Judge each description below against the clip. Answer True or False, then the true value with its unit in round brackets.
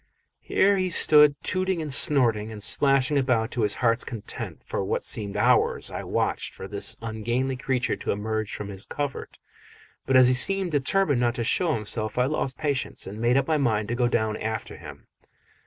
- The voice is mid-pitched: False (125 Hz)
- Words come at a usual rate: True (190 wpm)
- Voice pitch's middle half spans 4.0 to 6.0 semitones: True (4.6 semitones)